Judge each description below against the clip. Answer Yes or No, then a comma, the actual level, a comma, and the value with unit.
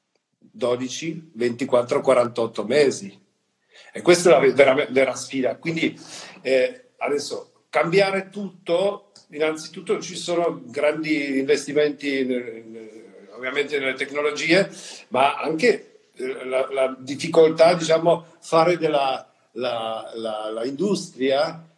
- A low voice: No, medium, 155 Hz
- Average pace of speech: No, slow, 105 wpm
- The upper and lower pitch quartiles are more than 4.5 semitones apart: Yes, average, 5.2 semitones